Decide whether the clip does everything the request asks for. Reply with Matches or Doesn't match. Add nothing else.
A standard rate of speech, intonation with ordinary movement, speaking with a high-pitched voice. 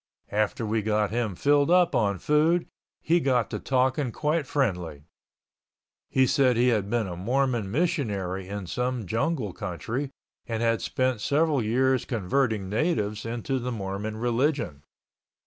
Doesn't match